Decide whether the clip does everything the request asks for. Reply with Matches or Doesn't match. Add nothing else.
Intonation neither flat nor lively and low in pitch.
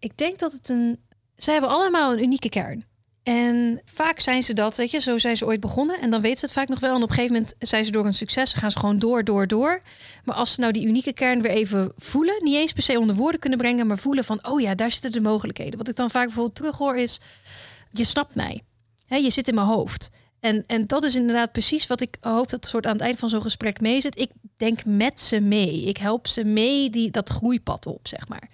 Doesn't match